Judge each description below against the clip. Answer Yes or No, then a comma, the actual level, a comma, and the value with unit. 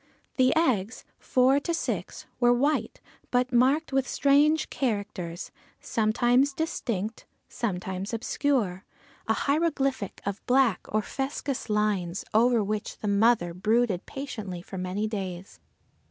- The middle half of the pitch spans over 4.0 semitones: Yes, average, 5.0 semitones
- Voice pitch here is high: Yes, high, 230 Hz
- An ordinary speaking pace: No, slow, 120 wpm